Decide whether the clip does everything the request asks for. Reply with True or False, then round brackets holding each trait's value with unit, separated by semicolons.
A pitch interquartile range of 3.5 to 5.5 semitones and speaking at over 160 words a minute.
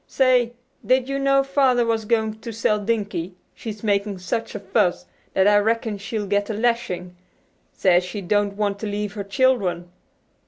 False (2.8 semitones; 170 wpm)